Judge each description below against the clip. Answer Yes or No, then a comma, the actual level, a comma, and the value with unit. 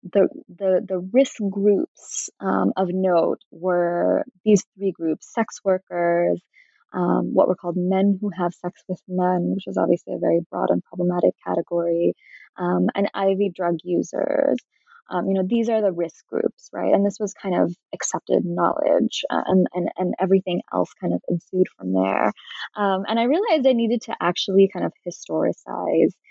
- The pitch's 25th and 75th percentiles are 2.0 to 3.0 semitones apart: Yes, narrow, 2.6 semitones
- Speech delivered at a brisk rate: No, average, 175 wpm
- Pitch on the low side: No, medium, 185 Hz